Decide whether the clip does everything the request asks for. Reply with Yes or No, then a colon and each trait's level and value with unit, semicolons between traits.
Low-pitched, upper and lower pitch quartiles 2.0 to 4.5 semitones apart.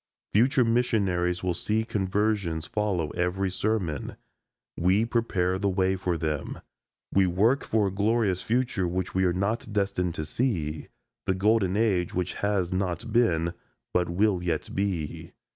Yes: very low, 95 Hz; average, 3.2 semitones